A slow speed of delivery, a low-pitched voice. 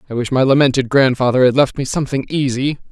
No: fast, 205 wpm; low, 130 Hz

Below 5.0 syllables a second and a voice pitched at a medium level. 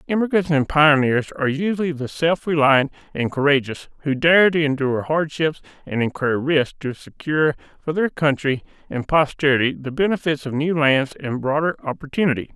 No: 5.4 syllables/s; medium, 145 Hz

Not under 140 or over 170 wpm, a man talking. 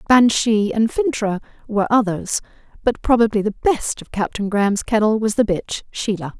No: average, 160 wpm; female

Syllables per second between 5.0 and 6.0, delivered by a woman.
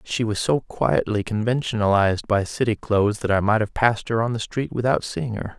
No: 5.5 syllables/s; male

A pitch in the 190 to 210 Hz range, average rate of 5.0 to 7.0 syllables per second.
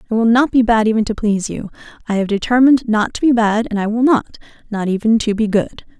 No: high, 225 Hz; 6.3 syllables/s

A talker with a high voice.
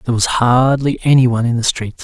No: low, 120 Hz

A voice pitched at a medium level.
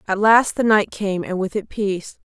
No: high, 200 Hz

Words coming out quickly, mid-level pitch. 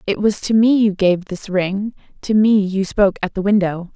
No: fast, 230 wpm; high, 200 Hz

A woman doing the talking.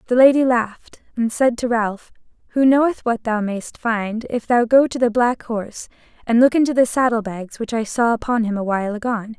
Yes: female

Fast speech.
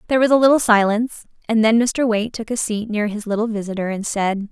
Yes: fast, 240 wpm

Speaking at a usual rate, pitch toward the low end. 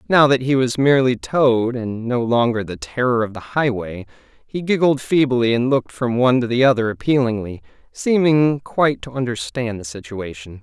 Yes: average, 175 wpm; low, 120 Hz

